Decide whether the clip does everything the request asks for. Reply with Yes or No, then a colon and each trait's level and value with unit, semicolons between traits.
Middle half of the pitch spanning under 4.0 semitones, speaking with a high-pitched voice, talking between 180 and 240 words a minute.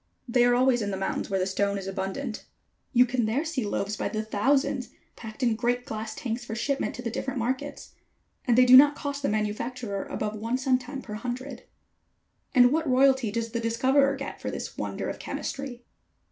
Yes: average, 3.4 semitones; high, 245 Hz; average, 200 wpm